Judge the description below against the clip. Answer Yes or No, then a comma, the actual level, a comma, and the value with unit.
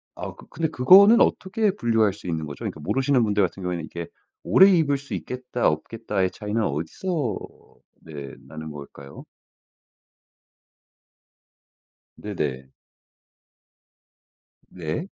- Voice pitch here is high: No, low, 105 Hz